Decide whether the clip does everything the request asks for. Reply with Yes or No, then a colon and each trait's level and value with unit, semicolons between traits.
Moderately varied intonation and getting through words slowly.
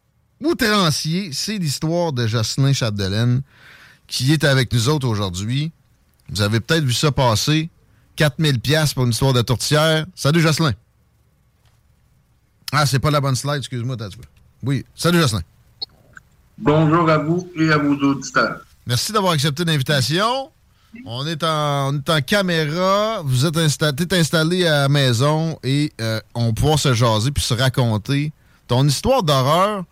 Yes: average, 4.2 semitones; slow, 140 wpm